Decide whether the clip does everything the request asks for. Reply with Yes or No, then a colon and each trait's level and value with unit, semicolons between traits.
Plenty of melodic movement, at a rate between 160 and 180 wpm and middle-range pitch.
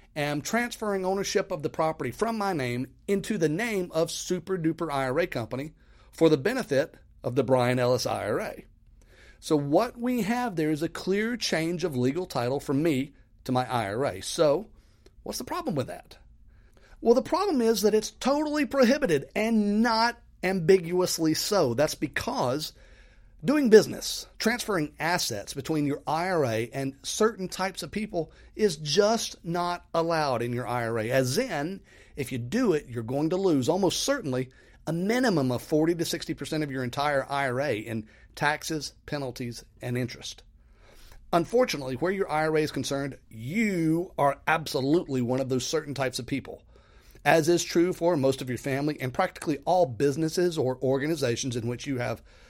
Yes: wide, 6.2 semitones; average, 165 wpm; medium, 155 Hz